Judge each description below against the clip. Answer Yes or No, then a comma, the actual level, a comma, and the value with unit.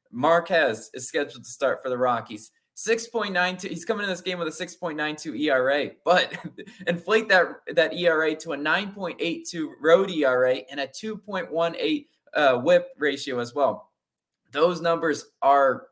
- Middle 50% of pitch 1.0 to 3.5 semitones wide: No, average, 4.7 semitones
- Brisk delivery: No, average, 190 wpm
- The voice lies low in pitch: No, medium, 170 Hz